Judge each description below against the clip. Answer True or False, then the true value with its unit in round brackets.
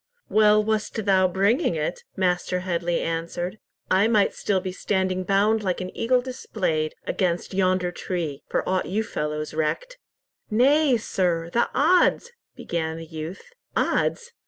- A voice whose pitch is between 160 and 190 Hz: True (185 Hz)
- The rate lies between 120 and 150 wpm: True (140 wpm)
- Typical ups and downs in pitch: True (4.1 semitones)